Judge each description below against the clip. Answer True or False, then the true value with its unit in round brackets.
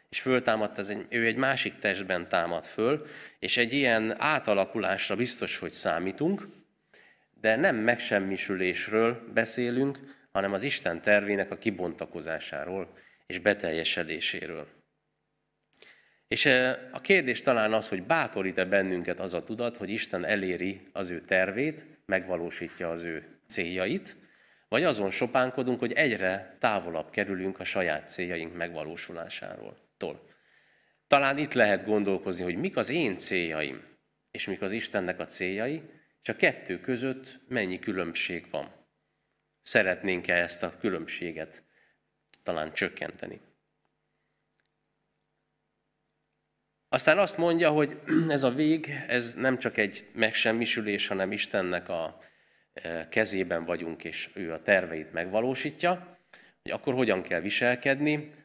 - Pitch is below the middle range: True (110 Hz)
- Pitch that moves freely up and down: True (5.8 semitones)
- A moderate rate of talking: True (120 wpm)